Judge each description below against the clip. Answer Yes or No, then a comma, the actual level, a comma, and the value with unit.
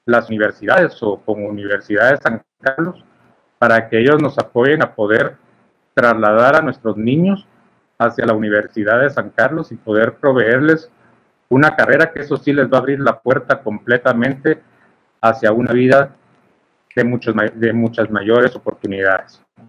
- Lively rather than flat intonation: No, average, 3.6 semitones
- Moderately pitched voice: No, low, 120 Hz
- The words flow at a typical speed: Yes, average, 150 wpm